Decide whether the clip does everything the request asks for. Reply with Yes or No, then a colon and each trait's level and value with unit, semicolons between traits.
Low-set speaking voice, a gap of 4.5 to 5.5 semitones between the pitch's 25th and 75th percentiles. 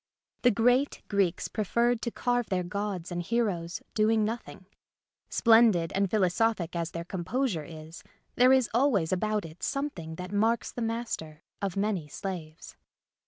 No: high, 200 Hz; average, 5.1 semitones